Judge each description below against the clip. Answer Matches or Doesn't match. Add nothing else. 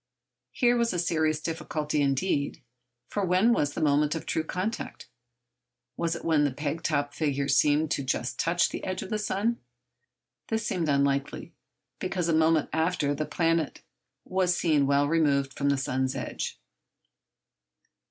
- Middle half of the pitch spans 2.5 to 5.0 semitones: Matches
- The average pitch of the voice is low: Doesn't match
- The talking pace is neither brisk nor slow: Matches